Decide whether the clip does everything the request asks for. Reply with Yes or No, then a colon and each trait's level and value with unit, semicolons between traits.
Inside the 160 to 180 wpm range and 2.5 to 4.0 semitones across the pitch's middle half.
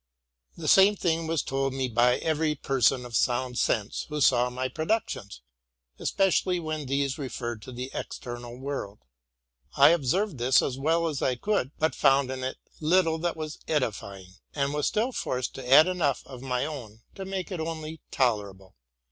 No: average, 175 wpm; average, 4.4 semitones